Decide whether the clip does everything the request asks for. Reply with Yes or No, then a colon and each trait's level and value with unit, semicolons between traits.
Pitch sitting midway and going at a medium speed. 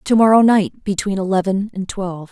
No: high, 200 Hz; average, 180 wpm